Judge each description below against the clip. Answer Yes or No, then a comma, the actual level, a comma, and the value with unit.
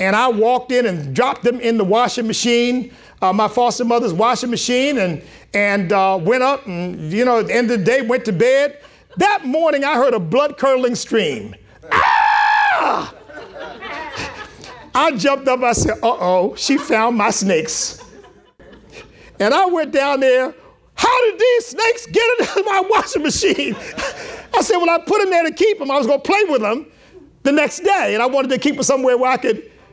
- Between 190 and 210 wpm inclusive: Yes, average, 195 wpm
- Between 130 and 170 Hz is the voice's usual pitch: No, very high, 255 Hz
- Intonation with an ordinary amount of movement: No, wide, 5.7 semitones